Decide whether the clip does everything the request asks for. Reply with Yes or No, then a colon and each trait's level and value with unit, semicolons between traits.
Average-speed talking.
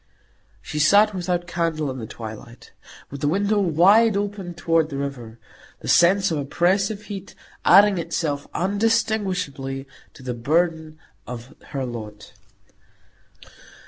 No: slow, 125 wpm